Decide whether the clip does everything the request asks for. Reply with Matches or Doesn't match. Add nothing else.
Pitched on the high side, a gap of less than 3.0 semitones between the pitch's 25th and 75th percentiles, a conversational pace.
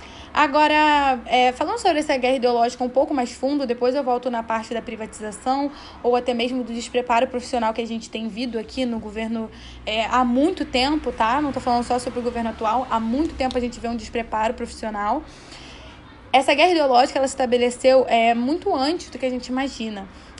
Doesn't match